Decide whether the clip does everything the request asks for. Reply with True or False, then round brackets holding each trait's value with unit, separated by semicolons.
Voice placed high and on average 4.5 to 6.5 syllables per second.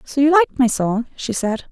True (255 Hz; 5.9 syllables/s)